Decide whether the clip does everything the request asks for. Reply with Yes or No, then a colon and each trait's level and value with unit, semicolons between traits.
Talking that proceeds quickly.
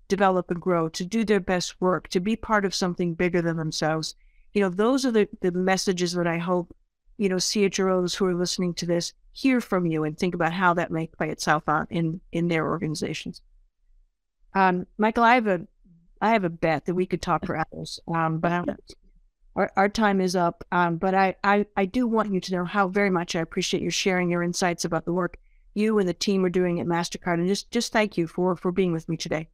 Yes: fast, 230 wpm